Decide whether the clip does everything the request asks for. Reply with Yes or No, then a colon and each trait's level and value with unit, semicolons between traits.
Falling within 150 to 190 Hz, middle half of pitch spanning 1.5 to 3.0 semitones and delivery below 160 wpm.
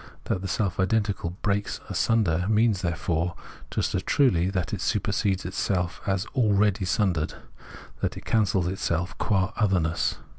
No: very low, 95 Hz; average, 2.7 semitones; average, 140 wpm